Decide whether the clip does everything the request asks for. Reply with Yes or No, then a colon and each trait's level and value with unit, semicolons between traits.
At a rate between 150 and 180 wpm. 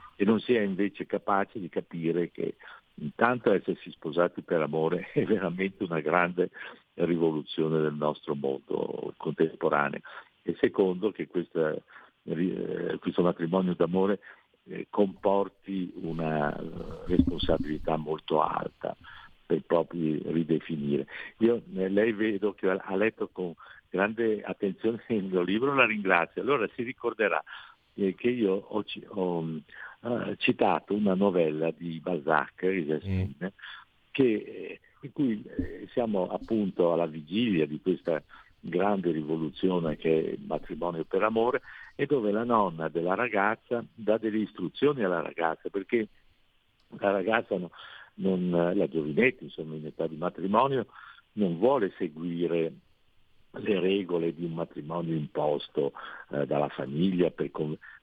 No: average, 120 wpm